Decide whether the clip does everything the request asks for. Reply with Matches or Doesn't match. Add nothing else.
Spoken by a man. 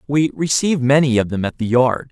Matches